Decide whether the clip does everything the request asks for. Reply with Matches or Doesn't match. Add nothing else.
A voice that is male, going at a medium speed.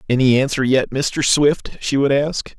Matches